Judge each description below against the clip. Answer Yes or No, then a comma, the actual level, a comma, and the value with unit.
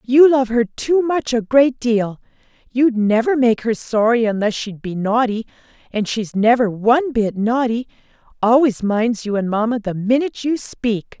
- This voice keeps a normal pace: Yes, average, 165 wpm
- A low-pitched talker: No, high, 235 Hz